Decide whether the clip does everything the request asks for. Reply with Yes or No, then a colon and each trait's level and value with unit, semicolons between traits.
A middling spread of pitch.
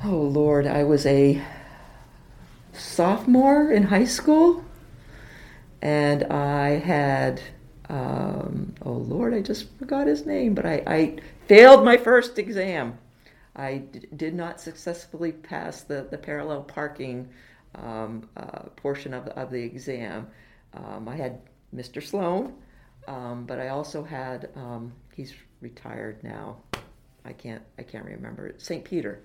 No: wide, 6.2 semitones